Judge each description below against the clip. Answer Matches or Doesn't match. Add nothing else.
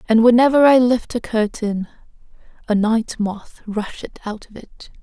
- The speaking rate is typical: Matches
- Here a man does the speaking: Doesn't match